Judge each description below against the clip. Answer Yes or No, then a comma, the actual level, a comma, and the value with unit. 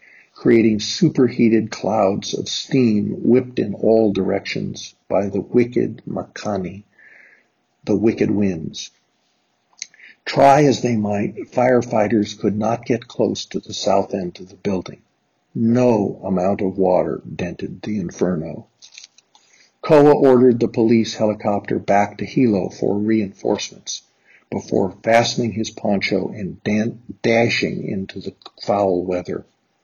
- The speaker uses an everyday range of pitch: Yes, average, 3.0 semitones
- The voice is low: Yes, low, 110 Hz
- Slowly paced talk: Yes, slow, 120 wpm